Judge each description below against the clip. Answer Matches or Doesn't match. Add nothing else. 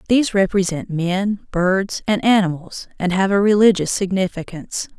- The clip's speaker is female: Matches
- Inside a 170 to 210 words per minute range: Doesn't match